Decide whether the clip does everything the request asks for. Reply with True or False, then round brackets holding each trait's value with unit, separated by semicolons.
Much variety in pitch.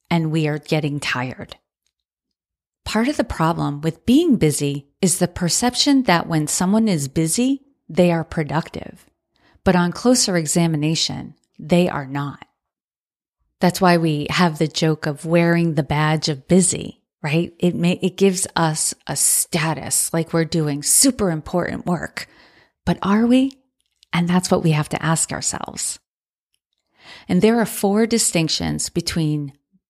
False (3.5 semitones)